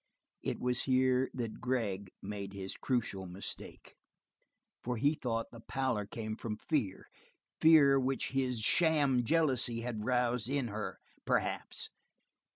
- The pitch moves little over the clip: No, average, 3.5 semitones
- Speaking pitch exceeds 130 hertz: No, low, 125 Hz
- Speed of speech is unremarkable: No, slow, 130 wpm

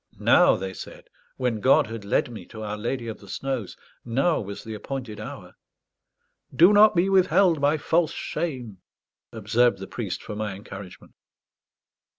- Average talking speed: Yes, average, 160 wpm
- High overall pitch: No, low, 115 Hz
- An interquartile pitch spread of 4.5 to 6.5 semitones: Yes, average, 5.3 semitones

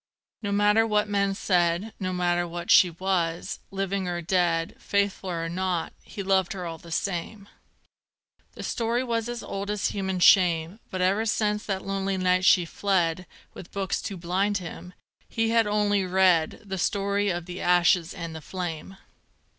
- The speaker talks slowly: No, average, 170 wpm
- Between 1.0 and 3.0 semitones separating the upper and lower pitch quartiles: Yes, narrow, 2.5 semitones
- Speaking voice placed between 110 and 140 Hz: No, high, 190 Hz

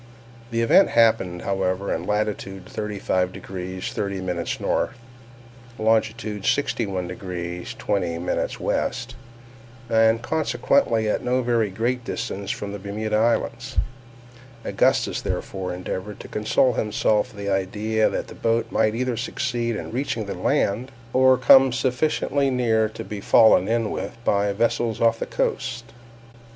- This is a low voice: Yes, low, 110 Hz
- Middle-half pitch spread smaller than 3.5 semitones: Yes, average, 3.1 semitones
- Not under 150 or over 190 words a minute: No, slow, 135 wpm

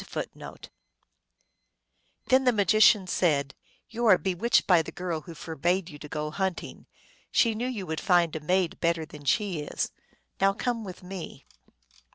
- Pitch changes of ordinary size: Yes, average, 4.4 semitones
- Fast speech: No, average, 165 wpm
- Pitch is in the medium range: Yes, medium, 180 Hz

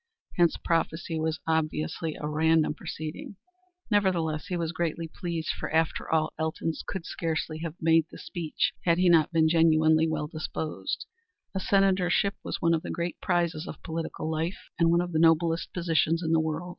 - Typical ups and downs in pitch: No, narrow, 1.4 semitones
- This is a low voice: No, medium, 165 Hz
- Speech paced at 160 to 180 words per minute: Yes, average, 175 wpm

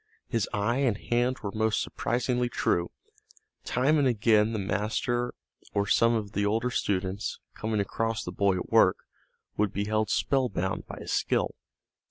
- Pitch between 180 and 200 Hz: No, low, 110 Hz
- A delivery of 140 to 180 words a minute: Yes, average, 160 wpm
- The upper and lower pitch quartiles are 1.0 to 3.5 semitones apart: Yes, average, 3.1 semitones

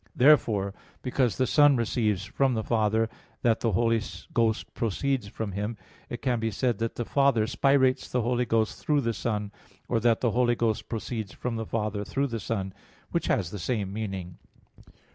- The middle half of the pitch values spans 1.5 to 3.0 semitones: Yes, narrow, 2.6 semitones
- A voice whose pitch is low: Yes, low, 115 Hz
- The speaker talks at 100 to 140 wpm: No, average, 180 wpm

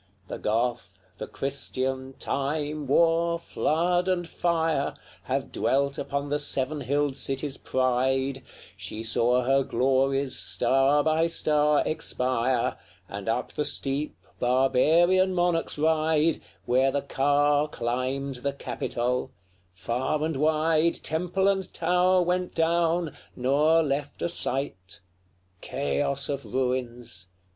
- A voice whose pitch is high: No, medium, 140 Hz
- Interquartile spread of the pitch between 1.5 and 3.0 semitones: No, average, 3.8 semitones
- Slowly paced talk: Yes, slow, 120 wpm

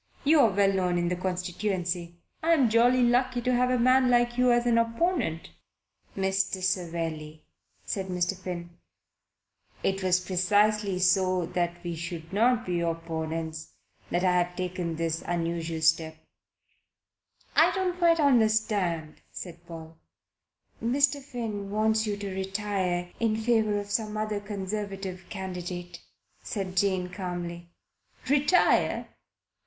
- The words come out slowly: Yes, slow, 130 wpm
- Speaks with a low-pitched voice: No, high, 190 Hz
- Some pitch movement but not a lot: Yes, average, 4.1 semitones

